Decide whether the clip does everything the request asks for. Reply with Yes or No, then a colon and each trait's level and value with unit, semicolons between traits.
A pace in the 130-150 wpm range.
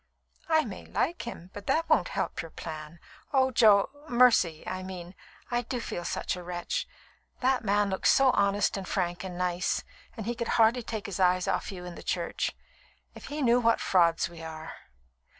No: average, 185 wpm